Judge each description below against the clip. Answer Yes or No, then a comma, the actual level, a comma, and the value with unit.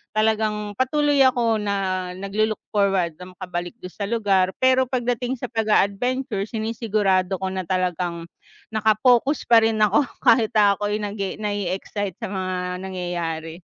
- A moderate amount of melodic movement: Yes, average, 3.1 semitones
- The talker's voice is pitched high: Yes, high, 205 Hz